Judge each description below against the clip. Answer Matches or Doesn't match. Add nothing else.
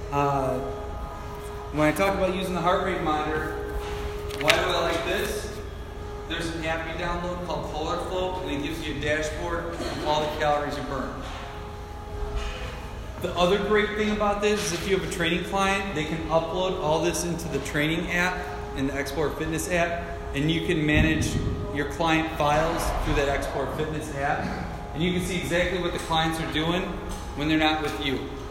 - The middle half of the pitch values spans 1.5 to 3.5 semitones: Doesn't match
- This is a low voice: Doesn't match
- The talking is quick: Doesn't match